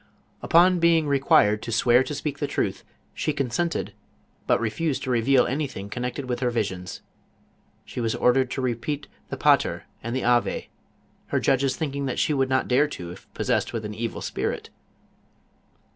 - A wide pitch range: No, average, 3.5 semitones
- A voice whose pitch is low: Yes, low, 130 Hz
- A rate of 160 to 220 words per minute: Yes, average, 170 wpm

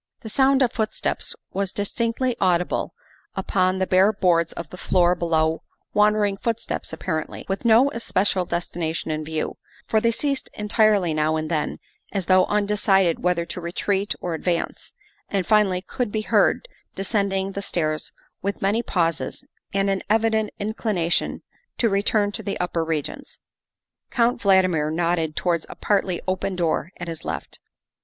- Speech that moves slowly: No, average, 150 wpm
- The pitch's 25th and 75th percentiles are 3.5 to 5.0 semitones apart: Yes, average, 3.8 semitones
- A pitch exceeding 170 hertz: Yes, high, 190 Hz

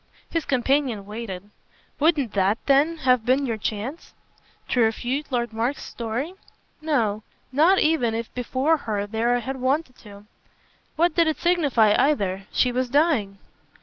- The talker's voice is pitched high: Yes, very high, 250 Hz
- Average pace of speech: Yes, average, 150 wpm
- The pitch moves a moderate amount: Yes, average, 4.9 semitones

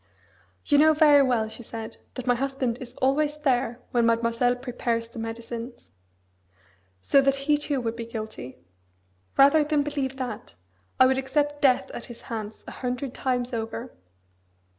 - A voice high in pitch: Yes, very high, 250 Hz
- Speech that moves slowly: No, average, 160 wpm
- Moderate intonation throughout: Yes, average, 3.0 semitones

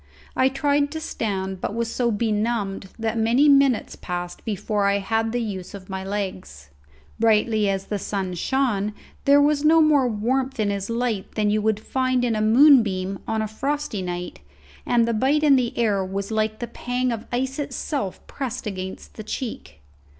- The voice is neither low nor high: No, high, 220 Hz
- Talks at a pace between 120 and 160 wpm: No, average, 180 wpm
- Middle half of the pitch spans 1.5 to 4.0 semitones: No, average, 4.4 semitones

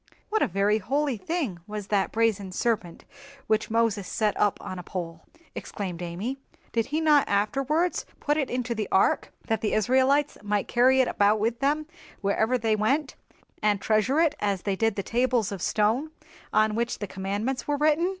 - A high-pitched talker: Yes, high, 220 Hz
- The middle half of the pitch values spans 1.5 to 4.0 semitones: No, average, 4.7 semitones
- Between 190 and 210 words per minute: No, average, 180 wpm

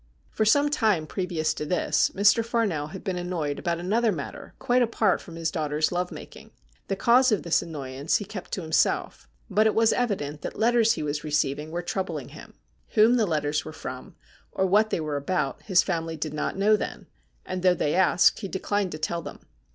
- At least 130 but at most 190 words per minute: No, fast, 205 wpm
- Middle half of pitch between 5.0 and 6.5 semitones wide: Yes, wide, 5.5 semitones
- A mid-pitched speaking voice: Yes, medium, 180 Hz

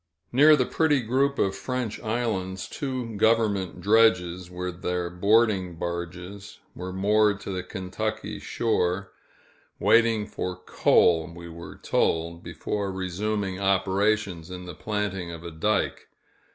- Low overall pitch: Yes, very low, 95 Hz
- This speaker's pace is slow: Yes, slow, 125 wpm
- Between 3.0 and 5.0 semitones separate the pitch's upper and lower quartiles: Yes, average, 3.4 semitones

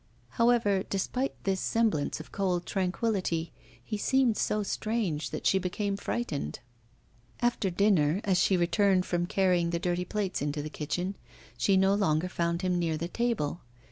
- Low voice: No, medium, 185 Hz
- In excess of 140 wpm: Yes, average, 155 wpm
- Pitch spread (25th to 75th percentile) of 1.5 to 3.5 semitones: Yes, average, 3.2 semitones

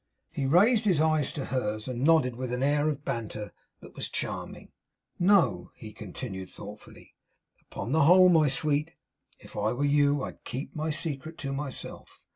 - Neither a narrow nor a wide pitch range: Yes, average, 4.2 semitones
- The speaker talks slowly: No, average, 170 wpm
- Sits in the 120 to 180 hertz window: Yes, medium, 140 Hz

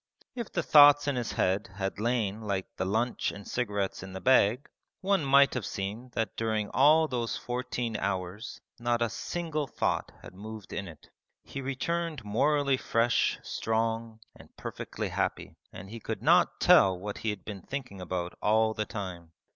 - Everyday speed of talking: Yes, average, 170 wpm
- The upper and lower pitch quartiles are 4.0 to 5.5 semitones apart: Yes, average, 4.8 semitones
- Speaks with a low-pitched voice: Yes, low, 115 Hz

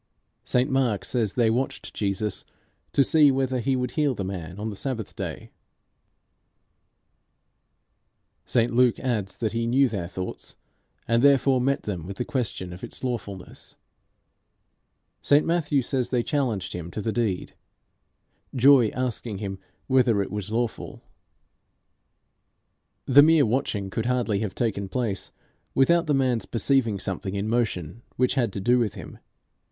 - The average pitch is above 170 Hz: No, low, 115 Hz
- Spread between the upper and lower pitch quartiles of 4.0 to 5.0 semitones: Yes, average, 4.5 semitones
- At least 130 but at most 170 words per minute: Yes, average, 145 wpm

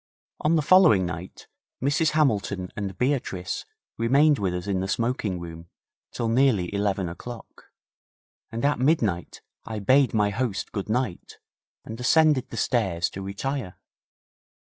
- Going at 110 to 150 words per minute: Yes, average, 140 wpm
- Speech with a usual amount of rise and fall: No, wide, 6.0 semitones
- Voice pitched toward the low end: Yes, low, 110 Hz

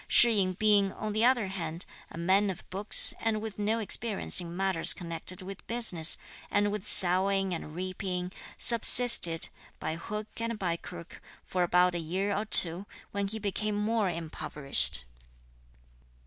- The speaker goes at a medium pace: Yes, average, 155 wpm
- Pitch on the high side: Yes, high, 195 Hz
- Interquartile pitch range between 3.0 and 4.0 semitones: Yes, average, 3.3 semitones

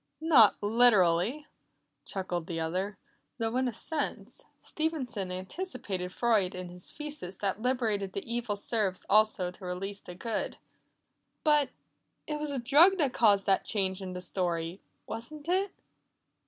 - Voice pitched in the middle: No, high, 210 Hz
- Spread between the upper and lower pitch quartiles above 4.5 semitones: Yes, wide, 5.5 semitones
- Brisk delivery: No, average, 140 wpm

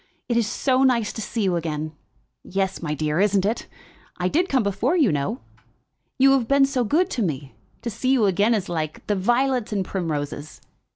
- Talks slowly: No, average, 195 wpm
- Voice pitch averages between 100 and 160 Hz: No, high, 205 Hz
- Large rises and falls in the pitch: Yes, wide, 6.5 semitones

